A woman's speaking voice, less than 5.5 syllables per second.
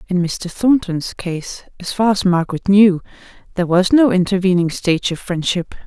Yes: female; 5.1 syllables/s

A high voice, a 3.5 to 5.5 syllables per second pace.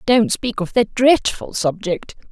Yes: high, 220 Hz; 3.9 syllables/s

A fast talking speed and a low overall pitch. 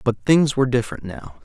Yes: fast, 210 wpm; low, 125 Hz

